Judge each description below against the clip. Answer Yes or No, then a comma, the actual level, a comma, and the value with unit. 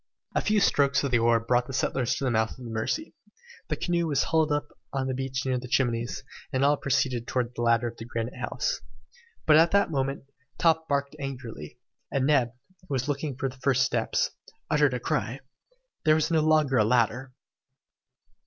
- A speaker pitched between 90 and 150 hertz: Yes, low, 135 Hz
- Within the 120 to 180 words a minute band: No, average, 195 wpm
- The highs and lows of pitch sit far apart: No, average, 3.3 semitones